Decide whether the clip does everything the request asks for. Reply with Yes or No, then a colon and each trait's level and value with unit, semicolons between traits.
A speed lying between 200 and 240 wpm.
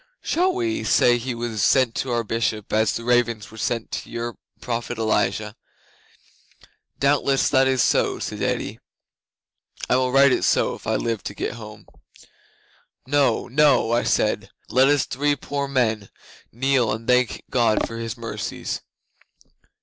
No: average, 155 wpm